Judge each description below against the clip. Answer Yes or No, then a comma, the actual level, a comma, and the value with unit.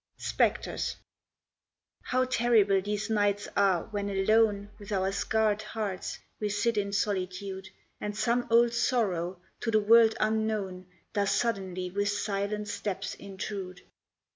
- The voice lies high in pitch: Yes, high, 205 Hz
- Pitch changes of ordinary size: No, narrow, 2.1 semitones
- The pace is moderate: No, slow, 125 wpm